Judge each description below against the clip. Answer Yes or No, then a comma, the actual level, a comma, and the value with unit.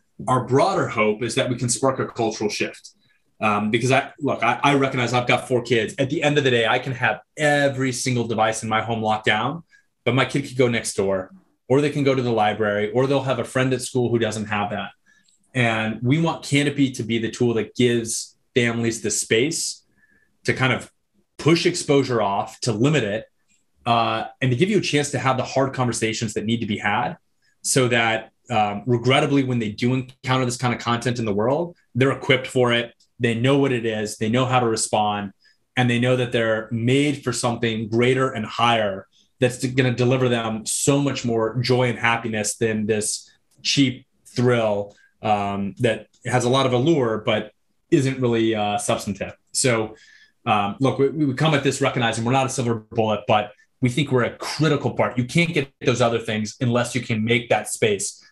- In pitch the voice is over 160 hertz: No, low, 120 Hz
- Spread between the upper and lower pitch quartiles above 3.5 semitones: No, average, 3.0 semitones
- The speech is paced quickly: Yes, fast, 210 wpm